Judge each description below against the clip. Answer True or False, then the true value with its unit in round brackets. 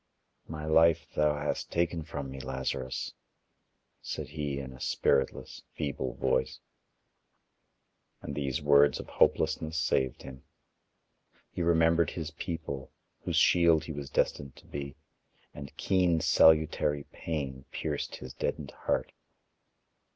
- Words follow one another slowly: True (120 wpm)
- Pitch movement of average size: True (3.2 semitones)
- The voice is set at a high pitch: False (75 Hz)